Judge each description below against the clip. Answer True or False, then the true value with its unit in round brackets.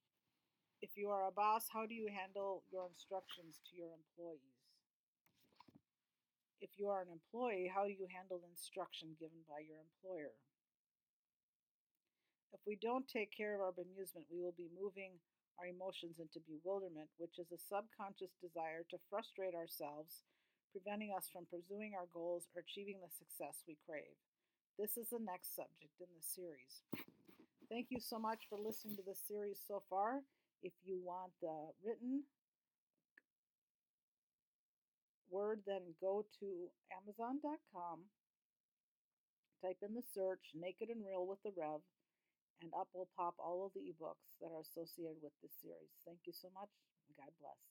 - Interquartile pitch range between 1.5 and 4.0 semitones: True (3.4 semitones)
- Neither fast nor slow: True (155 wpm)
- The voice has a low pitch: False (185 Hz)